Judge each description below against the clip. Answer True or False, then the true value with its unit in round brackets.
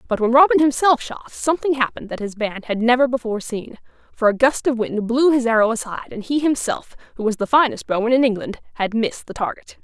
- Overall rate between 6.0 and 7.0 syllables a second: True (6.2 syllables/s)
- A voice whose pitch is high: True (245 Hz)